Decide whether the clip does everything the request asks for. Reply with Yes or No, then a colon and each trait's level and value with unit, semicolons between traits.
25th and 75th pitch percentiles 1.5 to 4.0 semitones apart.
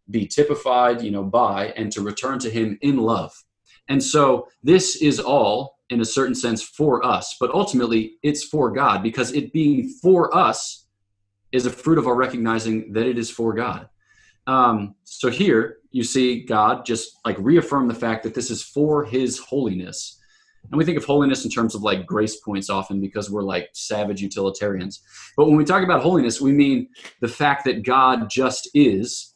No: average, 4.7 semitones